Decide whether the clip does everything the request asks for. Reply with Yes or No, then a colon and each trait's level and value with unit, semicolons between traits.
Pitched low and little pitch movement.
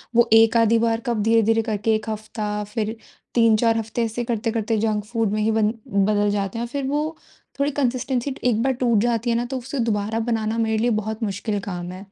No: high, 225 Hz; narrow, 1.8 semitones